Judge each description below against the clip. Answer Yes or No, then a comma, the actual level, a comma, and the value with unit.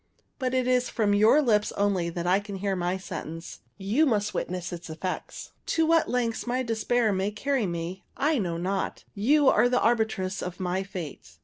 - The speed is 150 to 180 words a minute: No, average, 190 wpm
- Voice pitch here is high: Yes, high, 205 Hz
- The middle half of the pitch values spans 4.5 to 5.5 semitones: Yes, average, 5.1 semitones